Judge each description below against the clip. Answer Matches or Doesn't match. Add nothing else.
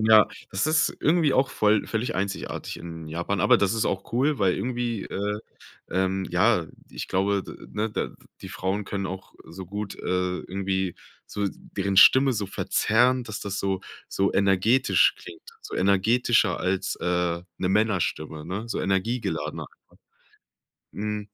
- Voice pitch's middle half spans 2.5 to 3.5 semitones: Matches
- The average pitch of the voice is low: Matches